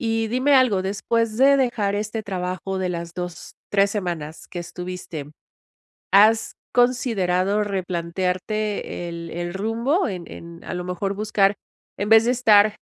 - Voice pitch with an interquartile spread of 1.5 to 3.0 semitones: No, average, 3.8 semitones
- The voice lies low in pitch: No, high, 200 Hz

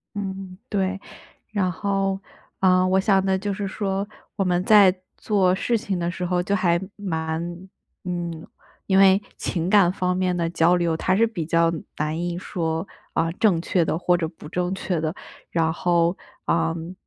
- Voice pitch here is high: No, medium, 180 Hz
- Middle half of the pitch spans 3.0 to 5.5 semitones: No, narrow, 2.4 semitones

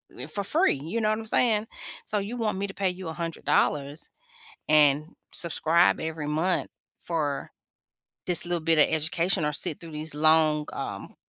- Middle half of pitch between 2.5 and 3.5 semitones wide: No, average, 4.1 semitones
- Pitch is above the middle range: No, medium, 165 Hz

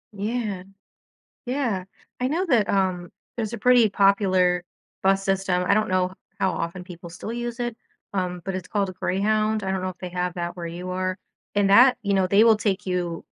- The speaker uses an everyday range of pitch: Yes, average, 3.0 semitones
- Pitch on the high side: Yes, high, 195 Hz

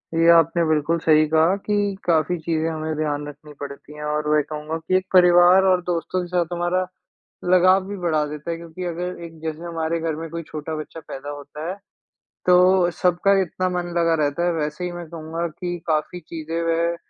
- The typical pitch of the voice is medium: Yes, medium, 165 Hz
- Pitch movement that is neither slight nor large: No, narrow, 2.2 semitones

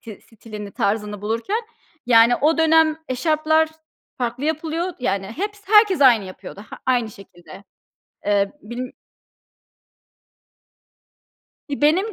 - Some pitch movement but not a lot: No, wide, 7.1 semitones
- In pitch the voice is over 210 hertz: Yes, very high, 255 Hz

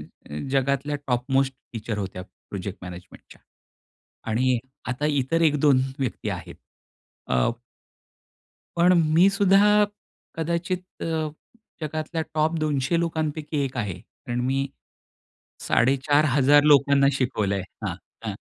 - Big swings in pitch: No, average, 4.2 semitones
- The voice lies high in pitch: No, medium, 140 Hz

